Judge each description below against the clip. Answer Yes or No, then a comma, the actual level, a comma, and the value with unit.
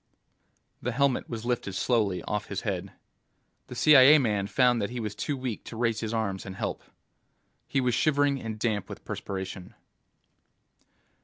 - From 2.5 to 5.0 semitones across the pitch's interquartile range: Yes, average, 3.8 semitones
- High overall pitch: No, low, 115 Hz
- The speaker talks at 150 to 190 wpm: Yes, average, 160 wpm